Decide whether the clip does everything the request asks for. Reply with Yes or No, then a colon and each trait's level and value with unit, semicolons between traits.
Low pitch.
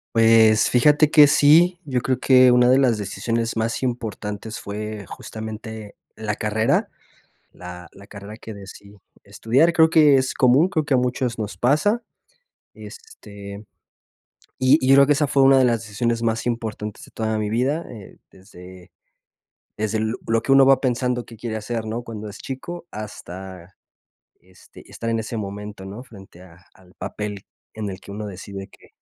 Yes: low, 115 Hz